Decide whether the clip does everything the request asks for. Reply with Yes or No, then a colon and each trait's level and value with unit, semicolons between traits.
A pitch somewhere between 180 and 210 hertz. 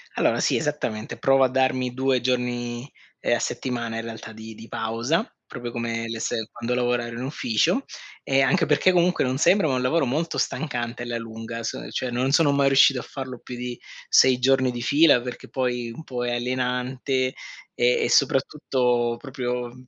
No: low, 125 Hz